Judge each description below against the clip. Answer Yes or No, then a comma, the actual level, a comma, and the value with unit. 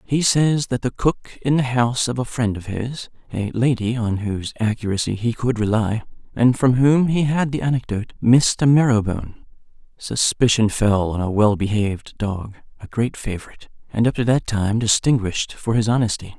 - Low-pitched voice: Yes, low, 115 Hz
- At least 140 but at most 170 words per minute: No, average, 185 wpm